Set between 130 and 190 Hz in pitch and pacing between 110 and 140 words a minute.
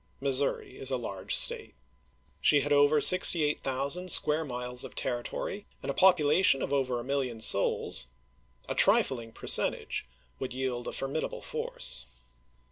Yes: low, 135 Hz; slow, 135 wpm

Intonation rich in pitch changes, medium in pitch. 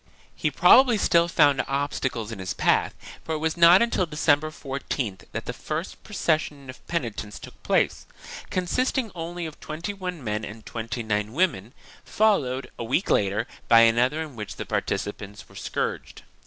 Yes: wide, 6.9 semitones; medium, 145 Hz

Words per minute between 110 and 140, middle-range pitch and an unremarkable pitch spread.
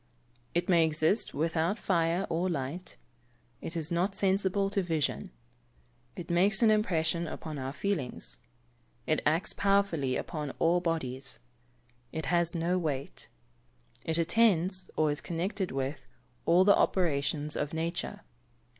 Yes: slow, 135 wpm; medium, 170 Hz; average, 3.2 semitones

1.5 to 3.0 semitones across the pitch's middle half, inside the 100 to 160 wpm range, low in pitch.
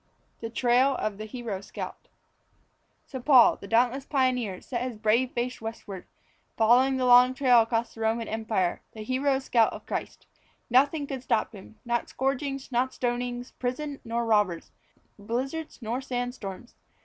No: average, 2.7 semitones; average, 155 wpm; high, 245 Hz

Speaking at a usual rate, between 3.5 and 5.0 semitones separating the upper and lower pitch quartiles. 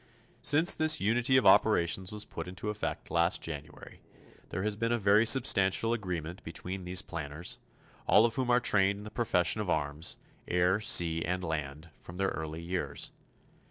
Yes: average, 170 wpm; average, 4.4 semitones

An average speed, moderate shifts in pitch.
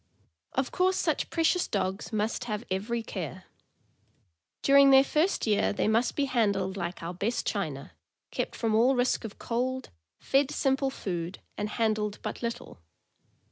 Yes: average, 150 wpm; average, 4.8 semitones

